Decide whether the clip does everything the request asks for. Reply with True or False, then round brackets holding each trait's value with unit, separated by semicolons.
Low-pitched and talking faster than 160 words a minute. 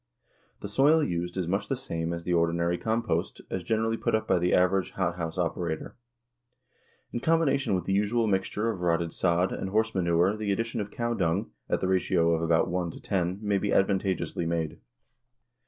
True (95 Hz; 190 wpm)